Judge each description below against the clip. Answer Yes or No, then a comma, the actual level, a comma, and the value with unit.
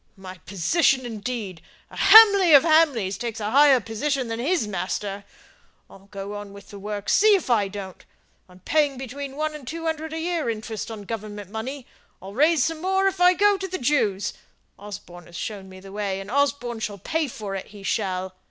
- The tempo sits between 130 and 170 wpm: No, average, 200 wpm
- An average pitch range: No, wide, 7.3 semitones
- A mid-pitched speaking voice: No, high, 225 Hz